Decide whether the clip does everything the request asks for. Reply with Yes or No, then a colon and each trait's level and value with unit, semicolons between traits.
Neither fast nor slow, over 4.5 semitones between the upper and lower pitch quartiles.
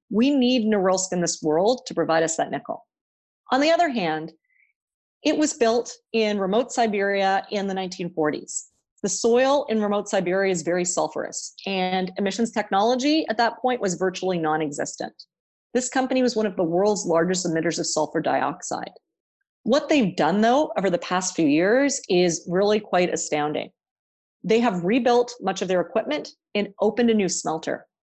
Yes: average, 165 wpm; average, 5.2 semitones